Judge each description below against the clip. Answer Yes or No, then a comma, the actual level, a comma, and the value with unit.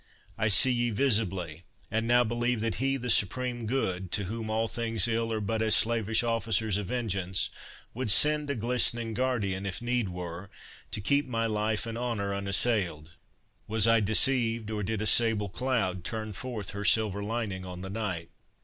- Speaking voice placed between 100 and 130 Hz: Yes, low, 110 Hz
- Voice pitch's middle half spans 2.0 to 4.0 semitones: Yes, average, 3.1 semitones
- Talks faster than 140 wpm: Yes, average, 175 wpm